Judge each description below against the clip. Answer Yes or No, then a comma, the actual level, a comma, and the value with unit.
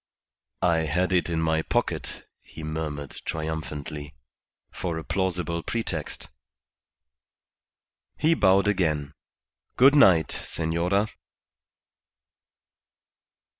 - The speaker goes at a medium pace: No, slow, 85 wpm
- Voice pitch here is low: Yes, very low, 85 Hz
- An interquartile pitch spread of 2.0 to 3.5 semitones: Yes, average, 3.1 semitones